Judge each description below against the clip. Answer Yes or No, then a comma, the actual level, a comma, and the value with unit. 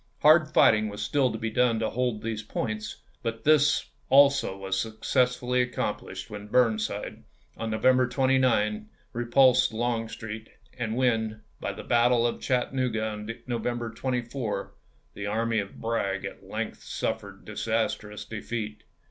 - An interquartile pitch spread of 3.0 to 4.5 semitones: No, narrow, 2.5 semitones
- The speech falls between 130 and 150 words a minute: Yes, average, 140 wpm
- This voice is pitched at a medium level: No, low, 115 Hz